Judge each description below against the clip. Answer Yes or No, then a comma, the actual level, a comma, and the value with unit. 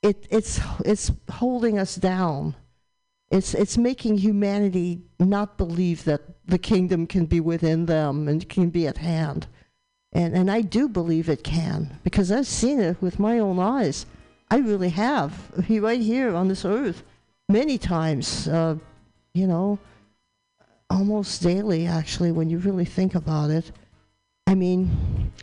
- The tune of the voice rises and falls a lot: No, average, 4.2 semitones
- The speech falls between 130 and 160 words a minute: Yes, average, 150 wpm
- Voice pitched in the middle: Yes, medium, 180 Hz